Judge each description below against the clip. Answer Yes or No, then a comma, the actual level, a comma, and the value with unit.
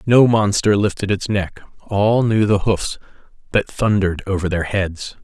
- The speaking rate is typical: Yes, average, 160 wpm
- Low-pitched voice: Yes, low, 100 Hz